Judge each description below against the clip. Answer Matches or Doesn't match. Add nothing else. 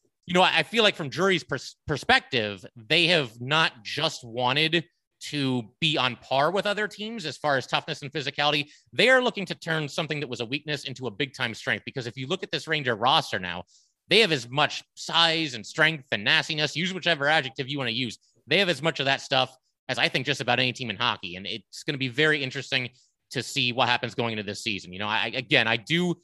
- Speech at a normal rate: Doesn't match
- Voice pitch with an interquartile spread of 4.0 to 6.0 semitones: Matches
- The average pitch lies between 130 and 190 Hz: Matches